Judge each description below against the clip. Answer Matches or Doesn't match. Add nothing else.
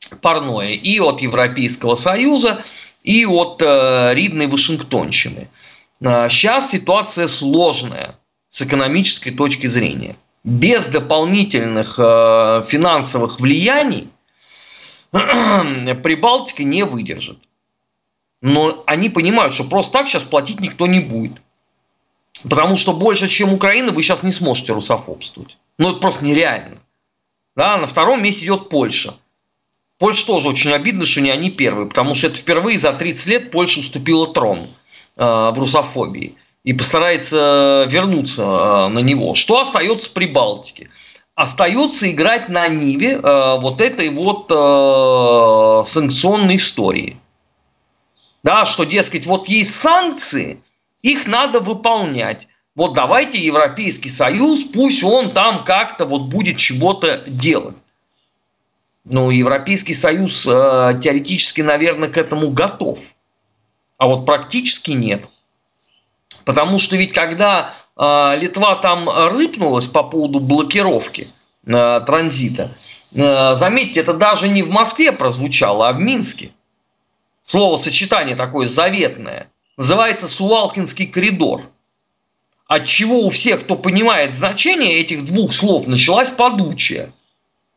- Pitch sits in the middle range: Matches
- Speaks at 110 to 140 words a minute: Matches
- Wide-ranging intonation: Matches